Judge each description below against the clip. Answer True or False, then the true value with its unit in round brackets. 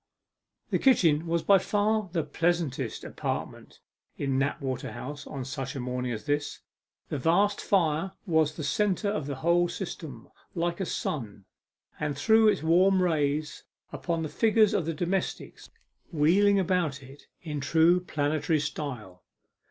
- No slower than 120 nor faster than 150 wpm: True (145 wpm)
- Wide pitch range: False (4.2 semitones)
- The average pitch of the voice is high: False (160 Hz)